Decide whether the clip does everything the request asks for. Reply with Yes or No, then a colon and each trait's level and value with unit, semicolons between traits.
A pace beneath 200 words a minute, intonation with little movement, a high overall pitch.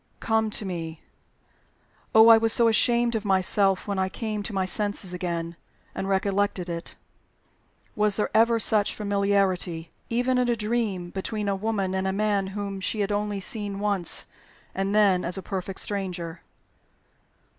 Yes: average, 160 wpm; narrow, 2.2 semitones; high, 200 Hz